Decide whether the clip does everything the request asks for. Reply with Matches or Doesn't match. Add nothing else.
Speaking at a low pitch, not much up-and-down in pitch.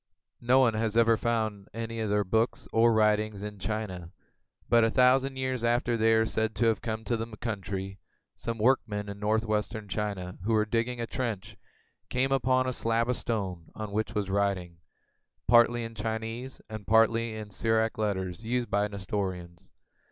Matches